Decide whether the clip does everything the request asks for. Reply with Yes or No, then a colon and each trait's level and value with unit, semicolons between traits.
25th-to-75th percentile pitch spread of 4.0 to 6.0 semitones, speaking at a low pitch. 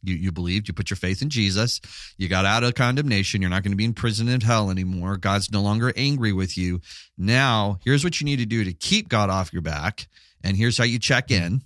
Yes: average, 4.3 semitones; low, 105 Hz